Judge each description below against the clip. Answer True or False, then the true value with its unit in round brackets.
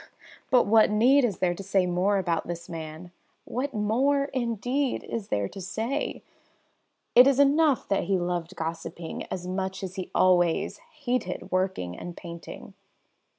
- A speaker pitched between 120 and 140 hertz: False (195 Hz)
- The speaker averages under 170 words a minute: True (150 wpm)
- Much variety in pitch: True (5.8 semitones)